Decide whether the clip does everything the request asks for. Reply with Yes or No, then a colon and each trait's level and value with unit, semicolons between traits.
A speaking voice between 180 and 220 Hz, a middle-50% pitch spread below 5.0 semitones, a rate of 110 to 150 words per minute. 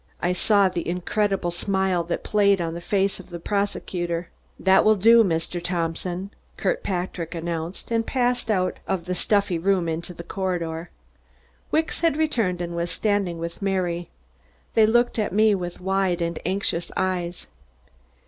No: medium, 185 Hz; average, 2.8 semitones; average, 160 wpm